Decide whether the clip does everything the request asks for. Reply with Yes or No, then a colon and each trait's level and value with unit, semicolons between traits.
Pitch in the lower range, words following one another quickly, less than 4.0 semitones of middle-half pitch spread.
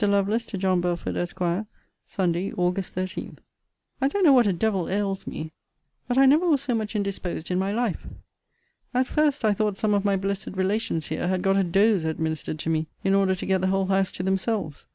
No: high, 195 Hz; fast, 210 wpm; average, 2.9 semitones